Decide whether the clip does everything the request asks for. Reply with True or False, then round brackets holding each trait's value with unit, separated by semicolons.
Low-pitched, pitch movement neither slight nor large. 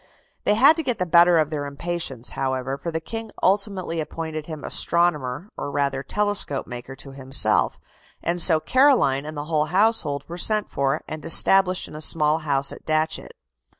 False (155 Hz; 4.5 semitones)